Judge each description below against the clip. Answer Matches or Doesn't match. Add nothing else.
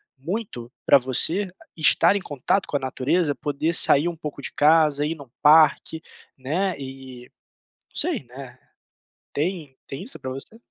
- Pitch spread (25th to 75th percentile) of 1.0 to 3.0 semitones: Doesn't match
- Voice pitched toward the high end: Doesn't match